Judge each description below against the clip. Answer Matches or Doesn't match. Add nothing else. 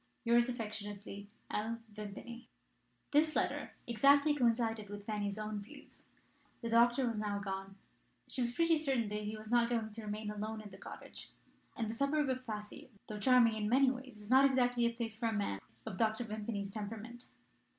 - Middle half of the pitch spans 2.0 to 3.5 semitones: Matches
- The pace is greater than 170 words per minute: Matches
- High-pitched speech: Matches